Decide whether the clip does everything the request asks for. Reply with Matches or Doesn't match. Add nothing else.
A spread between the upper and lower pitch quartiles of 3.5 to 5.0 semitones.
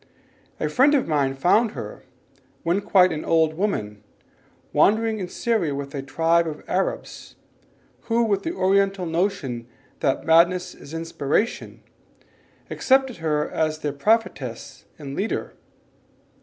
Doesn't match